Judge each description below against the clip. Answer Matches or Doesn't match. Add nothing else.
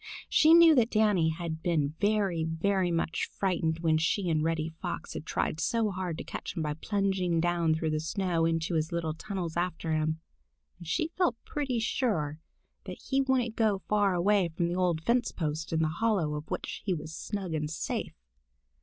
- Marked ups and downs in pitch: Doesn't match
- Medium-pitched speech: Matches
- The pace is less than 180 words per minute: Doesn't match